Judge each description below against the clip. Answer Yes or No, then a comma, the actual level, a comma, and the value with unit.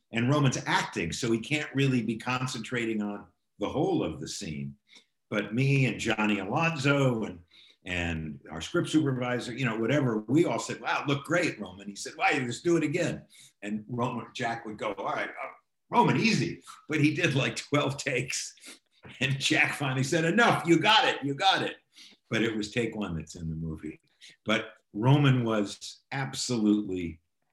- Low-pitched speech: Yes, low, 120 Hz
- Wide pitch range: Yes, wide, 5.7 semitones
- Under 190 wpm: Yes, average, 180 wpm